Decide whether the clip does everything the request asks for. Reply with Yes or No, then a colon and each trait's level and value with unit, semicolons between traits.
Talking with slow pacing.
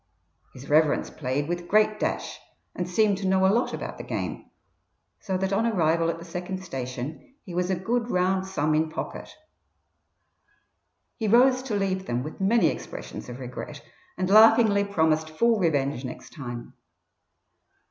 No: average, 160 wpm